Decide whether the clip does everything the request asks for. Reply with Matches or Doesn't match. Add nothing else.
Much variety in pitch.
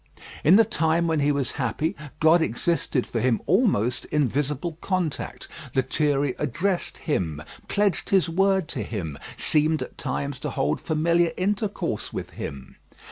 Doesn't match